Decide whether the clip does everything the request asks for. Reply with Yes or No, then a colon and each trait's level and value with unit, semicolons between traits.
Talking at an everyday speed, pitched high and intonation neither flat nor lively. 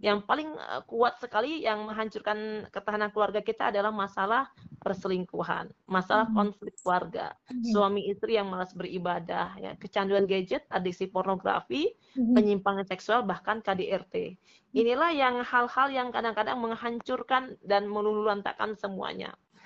Yes: average, 115 wpm; high, 210 Hz; average, 3.0 semitones